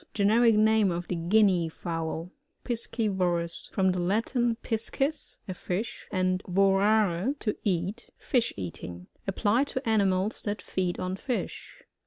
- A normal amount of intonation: Yes, average, 3.8 semitones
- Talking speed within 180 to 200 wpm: No, average, 140 wpm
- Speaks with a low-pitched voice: No, high, 195 Hz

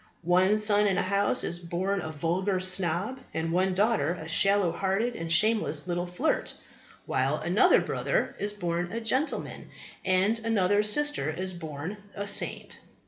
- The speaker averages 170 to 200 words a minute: No, average, 150 wpm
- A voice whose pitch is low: No, high, 190 Hz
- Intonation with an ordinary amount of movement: Yes, average, 3.3 semitones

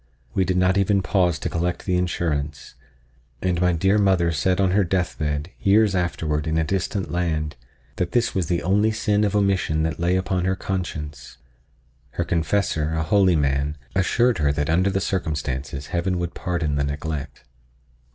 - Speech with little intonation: No, average, 3.5 semitones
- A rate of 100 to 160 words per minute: No, average, 175 wpm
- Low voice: Yes, very low, 90 Hz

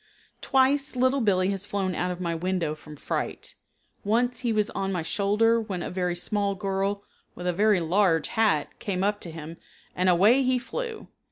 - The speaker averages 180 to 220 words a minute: Yes, average, 185 wpm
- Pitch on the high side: Yes, high, 195 Hz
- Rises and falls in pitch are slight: No, average, 3.9 semitones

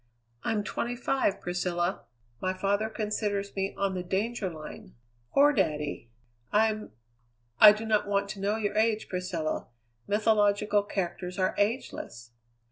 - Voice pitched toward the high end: Yes, high, 200 Hz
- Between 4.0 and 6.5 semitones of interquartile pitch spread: No, average, 2.9 semitones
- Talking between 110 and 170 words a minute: Yes, slow, 135 wpm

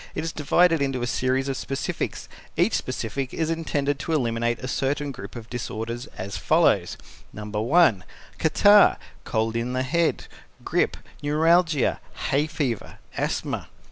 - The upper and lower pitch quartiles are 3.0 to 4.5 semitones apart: No, average, 4.9 semitones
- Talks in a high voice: No, low, 135 Hz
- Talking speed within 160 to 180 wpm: No, average, 140 wpm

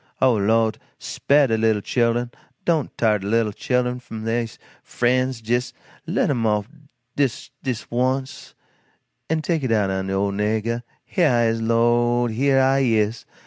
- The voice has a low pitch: Yes, low, 120 Hz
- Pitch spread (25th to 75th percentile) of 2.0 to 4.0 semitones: Yes, average, 2.7 semitones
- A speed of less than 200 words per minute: Yes, average, 160 wpm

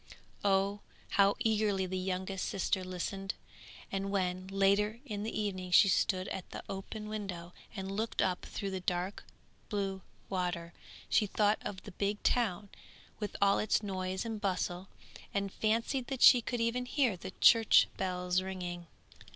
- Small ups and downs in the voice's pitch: Yes, narrow, 2.3 semitones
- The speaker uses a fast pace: No, average, 155 wpm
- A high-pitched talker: Yes, high, 195 Hz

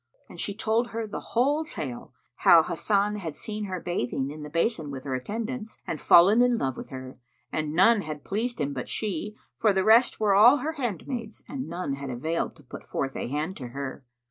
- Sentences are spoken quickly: Yes, fast, 210 wpm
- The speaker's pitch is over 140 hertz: Yes, high, 190 Hz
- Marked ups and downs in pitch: Yes, wide, 7.3 semitones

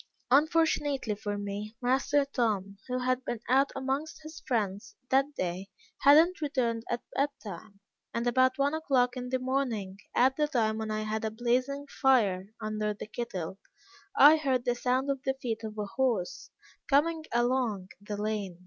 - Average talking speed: Yes, average, 170 wpm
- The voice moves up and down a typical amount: Yes, average, 4.2 semitones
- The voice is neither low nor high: No, high, 245 Hz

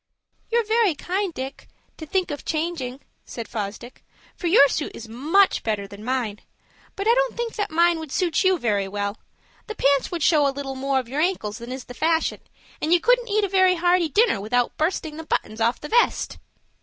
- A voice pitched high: Yes, very high, 310 Hz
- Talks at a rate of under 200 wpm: No, fast, 205 wpm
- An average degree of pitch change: No, wide, 7.1 semitones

